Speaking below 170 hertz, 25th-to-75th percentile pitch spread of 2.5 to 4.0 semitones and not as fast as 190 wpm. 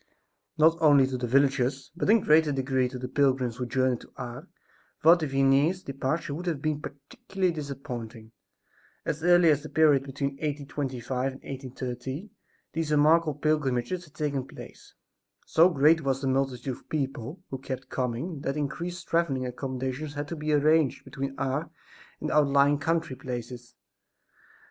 Yes: medium, 140 Hz; average, 2.9 semitones; average, 160 wpm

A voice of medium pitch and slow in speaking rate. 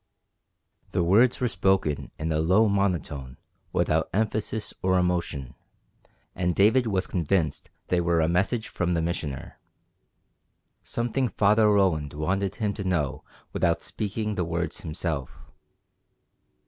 No: very low, 90 Hz; slow, 125 wpm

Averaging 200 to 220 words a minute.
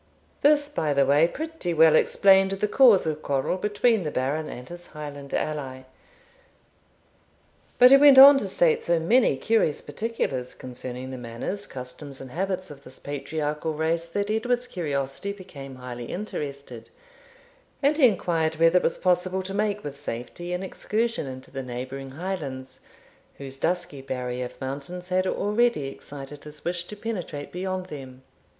No: average, 155 wpm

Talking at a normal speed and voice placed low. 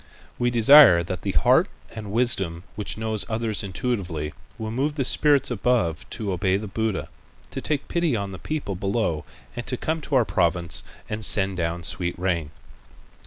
Yes: average, 170 wpm; low, 105 Hz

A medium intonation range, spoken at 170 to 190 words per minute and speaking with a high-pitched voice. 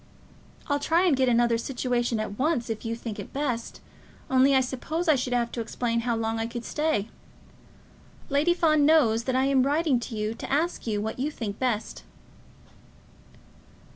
Yes: average, 3.8 semitones; average, 180 wpm; very high, 250 Hz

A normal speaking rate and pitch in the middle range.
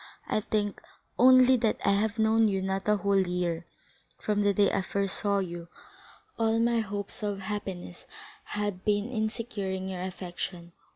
No: average, 165 wpm; high, 200 Hz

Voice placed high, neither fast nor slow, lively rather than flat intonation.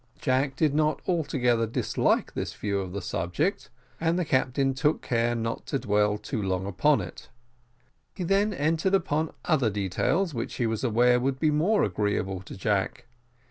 No: low, 130 Hz; average, 170 wpm; wide, 6.9 semitones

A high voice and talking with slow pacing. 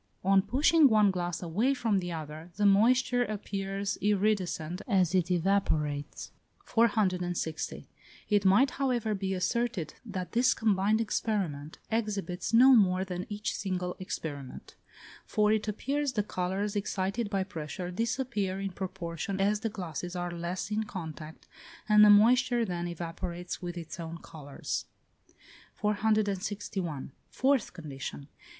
Yes: high, 195 Hz; slow, 130 wpm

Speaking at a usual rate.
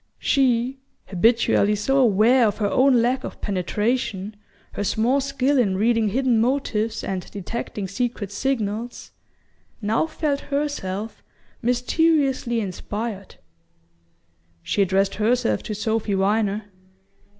No: slow, 110 wpm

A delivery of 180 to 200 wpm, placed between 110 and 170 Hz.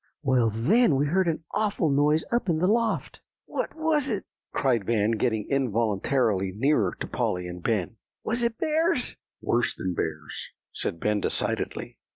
No: average, 160 wpm; low, 135 Hz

